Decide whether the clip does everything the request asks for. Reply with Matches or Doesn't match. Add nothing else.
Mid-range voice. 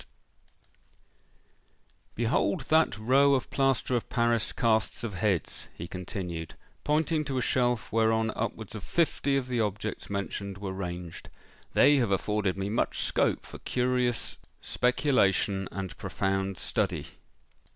Doesn't match